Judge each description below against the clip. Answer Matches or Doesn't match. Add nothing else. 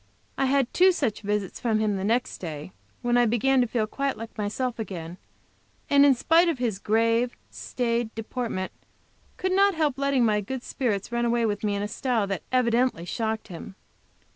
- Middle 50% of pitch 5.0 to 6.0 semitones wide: Doesn't match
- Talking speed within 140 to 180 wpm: Doesn't match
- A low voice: Doesn't match